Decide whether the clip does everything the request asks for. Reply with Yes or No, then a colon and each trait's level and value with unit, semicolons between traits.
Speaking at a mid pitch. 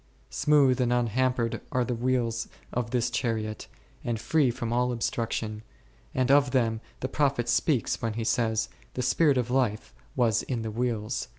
No: low, 120 Hz